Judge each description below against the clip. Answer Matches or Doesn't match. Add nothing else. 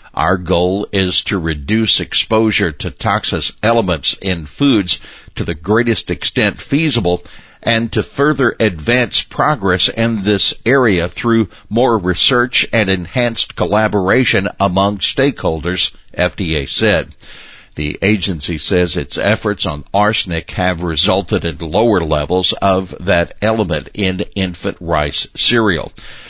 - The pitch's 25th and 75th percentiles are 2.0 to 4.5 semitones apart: Matches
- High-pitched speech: Doesn't match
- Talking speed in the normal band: Doesn't match